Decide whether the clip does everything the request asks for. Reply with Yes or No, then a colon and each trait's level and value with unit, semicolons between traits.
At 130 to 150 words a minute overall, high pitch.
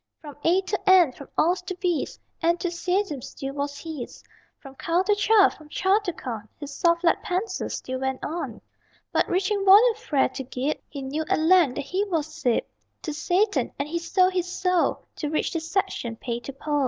No: average, 195 wpm; very high, 335 Hz